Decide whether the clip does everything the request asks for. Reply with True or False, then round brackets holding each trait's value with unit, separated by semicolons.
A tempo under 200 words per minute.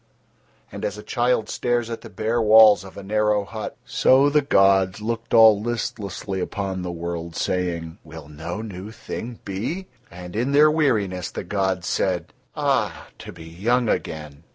True (165 wpm)